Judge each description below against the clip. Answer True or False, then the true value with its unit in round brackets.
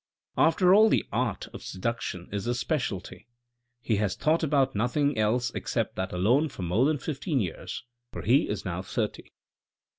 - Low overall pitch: True (120 Hz)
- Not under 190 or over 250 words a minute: False (175 wpm)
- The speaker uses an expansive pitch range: True (6.8 semitones)